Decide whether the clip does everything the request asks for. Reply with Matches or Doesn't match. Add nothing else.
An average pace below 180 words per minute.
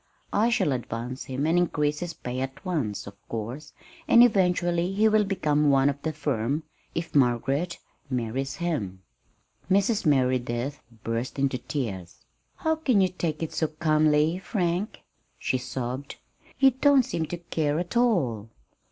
Matches